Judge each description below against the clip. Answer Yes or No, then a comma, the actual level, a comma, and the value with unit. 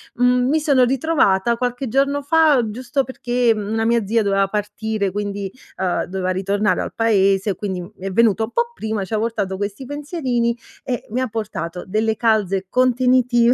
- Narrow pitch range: No, average, 4.0 semitones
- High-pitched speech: Yes, high, 225 Hz